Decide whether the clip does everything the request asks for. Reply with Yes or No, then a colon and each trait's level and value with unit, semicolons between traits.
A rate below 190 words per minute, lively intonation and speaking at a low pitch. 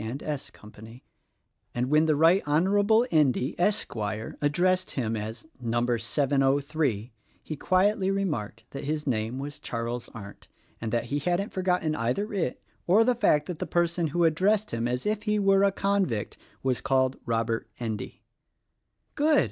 No: average, 160 wpm; wide, 7.7 semitones; medium, 145 Hz